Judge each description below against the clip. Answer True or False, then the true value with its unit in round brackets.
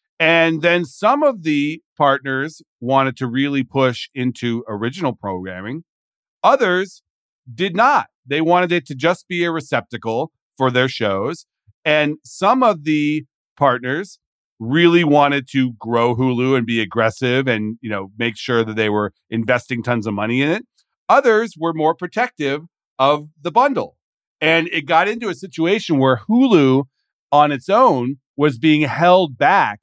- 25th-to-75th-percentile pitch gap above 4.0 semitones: True (5.0 semitones)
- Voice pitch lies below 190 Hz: True (140 Hz)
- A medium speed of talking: True (155 wpm)